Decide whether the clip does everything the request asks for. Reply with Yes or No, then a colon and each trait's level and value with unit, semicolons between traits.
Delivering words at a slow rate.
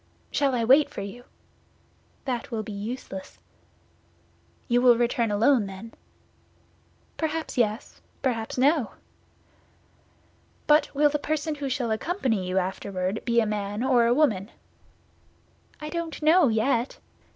Yes: slow, 130 wpm